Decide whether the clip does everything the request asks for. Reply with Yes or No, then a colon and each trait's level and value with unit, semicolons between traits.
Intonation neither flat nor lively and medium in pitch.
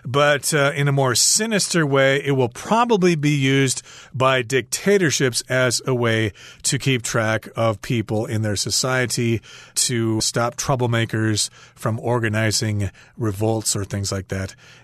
No: average, 4.0 semitones; low, 125 Hz